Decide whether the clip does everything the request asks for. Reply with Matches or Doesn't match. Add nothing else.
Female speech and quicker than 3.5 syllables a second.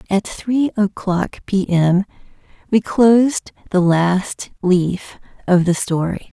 Doesn't match